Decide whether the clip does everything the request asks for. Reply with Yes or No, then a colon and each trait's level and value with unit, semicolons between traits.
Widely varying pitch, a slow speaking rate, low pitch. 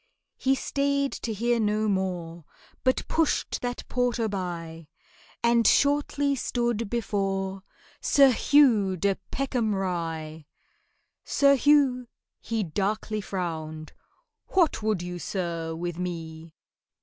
No: wide, 6.0 semitones; slow, 110 wpm; high, 205 Hz